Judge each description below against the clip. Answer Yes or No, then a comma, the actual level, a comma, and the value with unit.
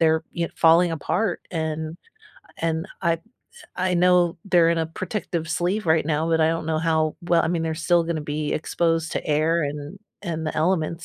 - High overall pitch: No, medium, 165 Hz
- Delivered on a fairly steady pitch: Yes, narrow, 1.4 semitones